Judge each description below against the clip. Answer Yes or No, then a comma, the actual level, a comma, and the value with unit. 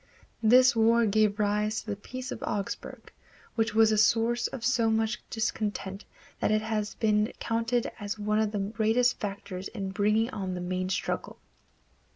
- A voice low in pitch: No, high, 215 Hz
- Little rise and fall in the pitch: Yes, narrow, 1.8 semitones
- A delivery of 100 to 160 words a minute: No, average, 170 wpm